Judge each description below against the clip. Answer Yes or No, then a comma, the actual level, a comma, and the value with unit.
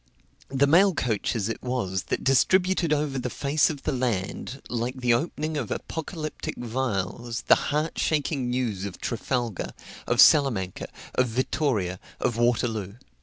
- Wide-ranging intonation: No, average, 4.3 semitones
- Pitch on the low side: Yes, low, 125 Hz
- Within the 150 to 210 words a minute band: No, average, 140 wpm